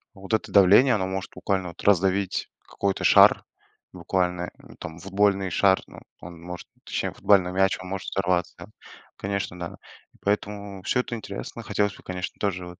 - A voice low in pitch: Yes, very low, 95 Hz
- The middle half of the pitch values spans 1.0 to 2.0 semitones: Yes, narrow, 1.7 semitones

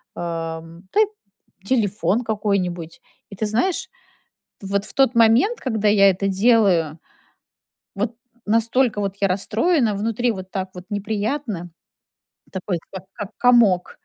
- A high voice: Yes, high, 205 Hz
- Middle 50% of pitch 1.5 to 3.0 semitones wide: No, average, 3.6 semitones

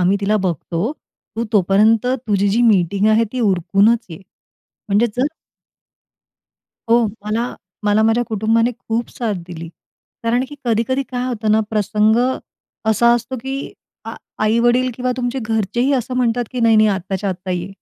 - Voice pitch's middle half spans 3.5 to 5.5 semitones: No, average, 3.1 semitones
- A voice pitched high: Yes, high, 225 Hz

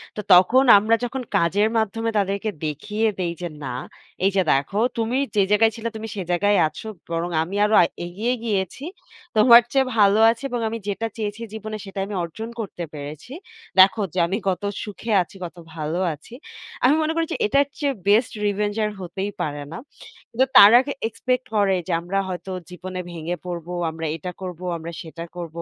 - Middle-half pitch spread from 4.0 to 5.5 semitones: Yes, average, 4.3 semitones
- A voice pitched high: Yes, high, 200 Hz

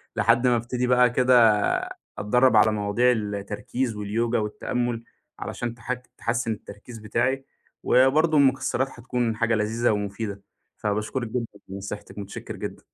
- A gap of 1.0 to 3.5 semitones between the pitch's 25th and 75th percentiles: Yes, average, 2.8 semitones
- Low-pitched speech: Yes, low, 115 Hz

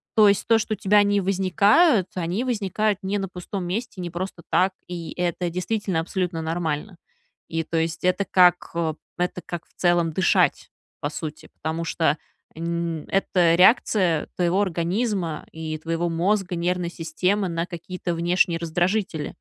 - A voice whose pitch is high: No, medium, 180 Hz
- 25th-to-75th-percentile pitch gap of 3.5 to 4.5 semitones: No, average, 2.7 semitones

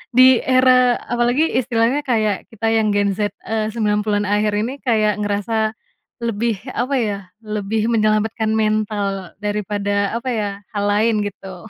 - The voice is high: Yes, high, 215 Hz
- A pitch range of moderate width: No, narrow, 2.1 semitones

